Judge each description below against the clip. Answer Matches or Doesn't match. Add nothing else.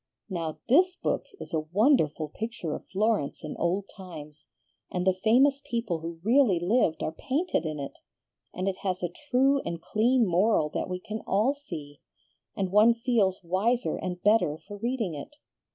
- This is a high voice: Matches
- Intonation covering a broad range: Matches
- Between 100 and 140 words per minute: Doesn't match